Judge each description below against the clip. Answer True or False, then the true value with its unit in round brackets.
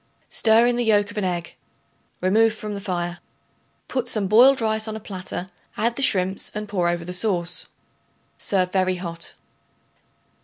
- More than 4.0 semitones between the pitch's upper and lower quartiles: False (3.4 semitones)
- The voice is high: True (200 Hz)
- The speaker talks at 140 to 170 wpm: True (165 wpm)